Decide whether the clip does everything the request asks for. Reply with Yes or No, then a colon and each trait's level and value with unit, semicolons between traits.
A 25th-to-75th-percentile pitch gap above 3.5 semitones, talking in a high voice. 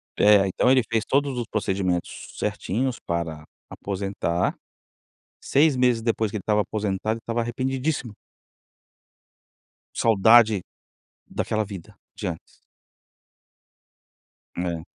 No: average, 4.0 semitones; low, 110 Hz